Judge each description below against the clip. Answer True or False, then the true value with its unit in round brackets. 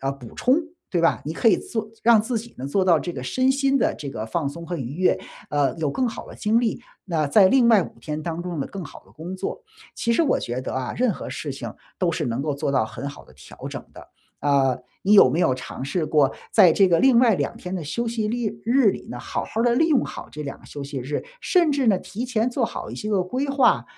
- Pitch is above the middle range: False (180 Hz)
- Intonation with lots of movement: True (8.4 semitones)